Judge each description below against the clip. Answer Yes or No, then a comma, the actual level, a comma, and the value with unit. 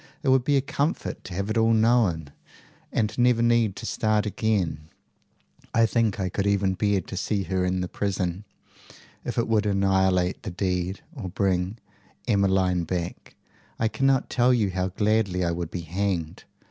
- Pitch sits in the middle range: No, low, 100 Hz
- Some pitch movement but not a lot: Yes, average, 3.4 semitones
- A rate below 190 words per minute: Yes, average, 170 wpm